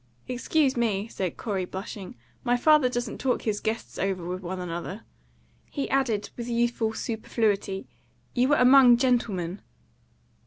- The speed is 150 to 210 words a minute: No, average, 140 wpm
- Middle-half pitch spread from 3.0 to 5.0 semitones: Yes, average, 4.3 semitones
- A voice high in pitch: Yes, high, 225 Hz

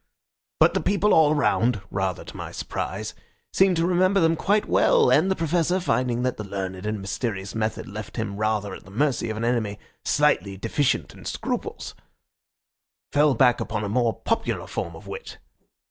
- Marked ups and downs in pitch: Yes, wide, 7.6 semitones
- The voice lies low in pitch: Yes, low, 120 Hz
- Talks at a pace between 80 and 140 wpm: No, average, 175 wpm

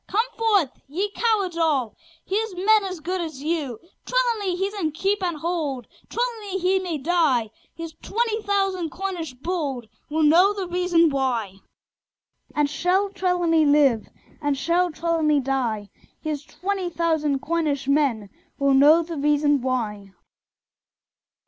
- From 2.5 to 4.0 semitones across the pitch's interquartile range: No, average, 5.1 semitones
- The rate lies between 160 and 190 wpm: No, slow, 135 wpm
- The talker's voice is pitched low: No, very high, 330 Hz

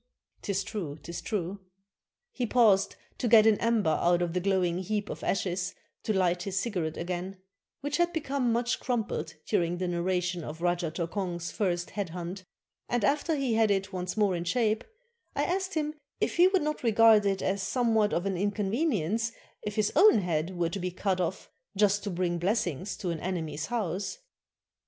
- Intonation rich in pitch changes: No, average, 4.2 semitones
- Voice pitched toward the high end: Yes, high, 195 Hz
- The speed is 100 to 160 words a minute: No, average, 190 wpm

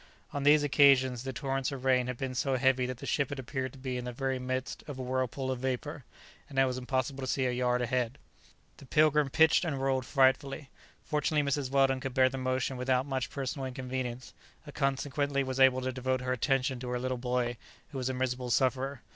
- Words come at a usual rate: No, fast, 220 wpm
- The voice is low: Yes, low, 130 Hz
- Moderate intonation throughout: No, narrow, 1.3 semitones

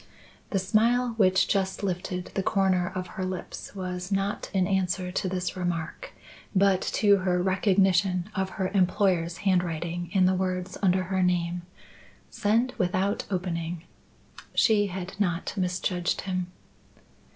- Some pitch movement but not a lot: No, narrow, 1.5 semitones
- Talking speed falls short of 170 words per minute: Yes, slow, 135 wpm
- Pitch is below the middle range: No, medium, 185 Hz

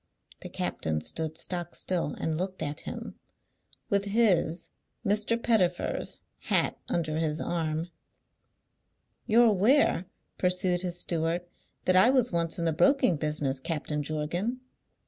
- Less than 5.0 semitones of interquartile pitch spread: Yes, average, 4.2 semitones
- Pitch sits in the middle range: Yes, medium, 175 Hz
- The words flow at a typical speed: No, slow, 125 wpm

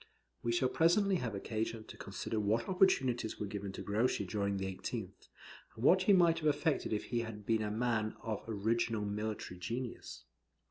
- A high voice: No, low, 115 Hz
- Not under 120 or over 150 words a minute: No, average, 180 wpm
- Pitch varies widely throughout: No, average, 3.5 semitones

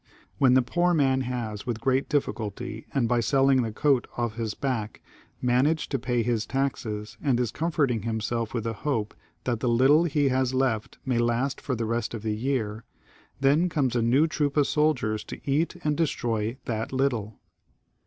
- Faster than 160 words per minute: Yes, average, 185 wpm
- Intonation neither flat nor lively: Yes, average, 3.3 semitones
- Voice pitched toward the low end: Yes, low, 125 Hz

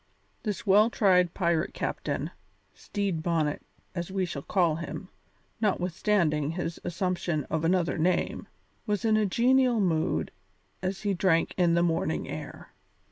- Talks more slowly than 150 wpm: Yes, slow, 135 wpm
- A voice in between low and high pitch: Yes, medium, 180 Hz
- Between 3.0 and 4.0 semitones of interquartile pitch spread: Yes, average, 3.3 semitones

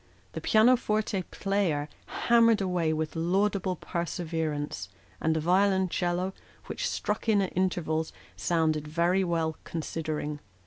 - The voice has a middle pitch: Yes, medium, 175 Hz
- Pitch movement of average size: Yes, average, 3.6 semitones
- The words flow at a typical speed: No, slow, 120 wpm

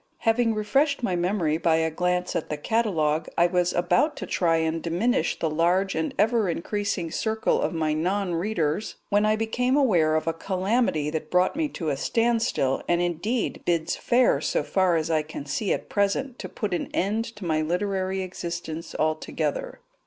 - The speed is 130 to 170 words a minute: No, average, 180 wpm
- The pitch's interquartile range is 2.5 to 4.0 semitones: No, average, 5.0 semitones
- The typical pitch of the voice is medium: Yes, medium, 180 Hz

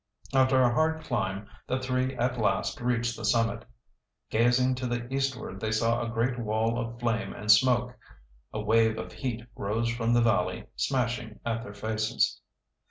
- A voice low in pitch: Yes, low, 115 Hz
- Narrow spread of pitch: Yes, narrow, 1.9 semitones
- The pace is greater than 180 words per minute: No, average, 165 wpm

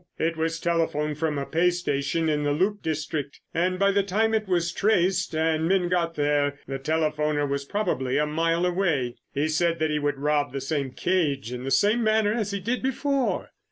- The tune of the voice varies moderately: Yes, average, 4.0 semitones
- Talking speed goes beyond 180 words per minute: Yes, average, 200 wpm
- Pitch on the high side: No, medium, 160 Hz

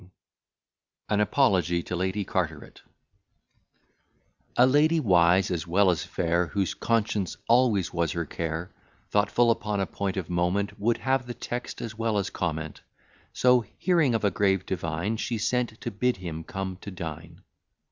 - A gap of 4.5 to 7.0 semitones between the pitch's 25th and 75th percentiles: Yes, average, 4.8 semitones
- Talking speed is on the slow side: No, average, 155 wpm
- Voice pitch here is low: Yes, low, 100 Hz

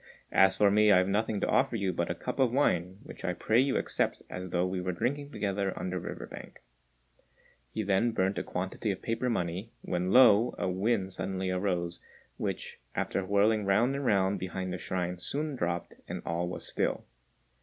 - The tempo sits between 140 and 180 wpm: No, average, 195 wpm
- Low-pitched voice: Yes, very low, 95 Hz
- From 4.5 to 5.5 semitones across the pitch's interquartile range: No, average, 3.5 semitones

